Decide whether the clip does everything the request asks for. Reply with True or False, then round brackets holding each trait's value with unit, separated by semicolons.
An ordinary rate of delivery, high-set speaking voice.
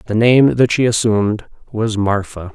False (165 wpm; 110 Hz)